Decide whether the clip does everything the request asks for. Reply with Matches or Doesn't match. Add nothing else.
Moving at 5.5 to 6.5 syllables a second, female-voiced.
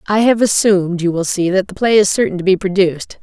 Matches